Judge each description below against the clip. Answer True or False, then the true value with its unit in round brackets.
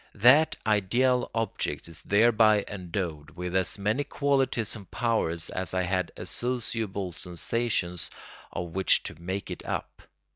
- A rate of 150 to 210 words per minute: False (135 wpm)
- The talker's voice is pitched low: True (100 Hz)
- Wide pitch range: False (4.6 semitones)